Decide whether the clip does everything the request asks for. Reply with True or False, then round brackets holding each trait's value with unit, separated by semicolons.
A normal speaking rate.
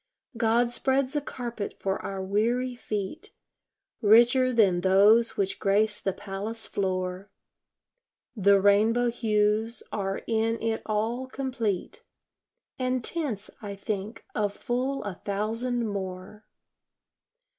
False (115 wpm)